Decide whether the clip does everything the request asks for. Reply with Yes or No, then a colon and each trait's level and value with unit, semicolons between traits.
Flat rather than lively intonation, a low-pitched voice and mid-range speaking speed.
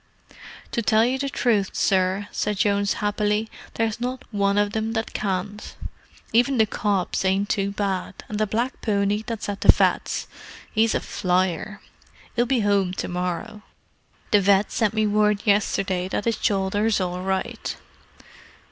No: narrow, 2.2 semitones; high, 205 Hz; average, 155 wpm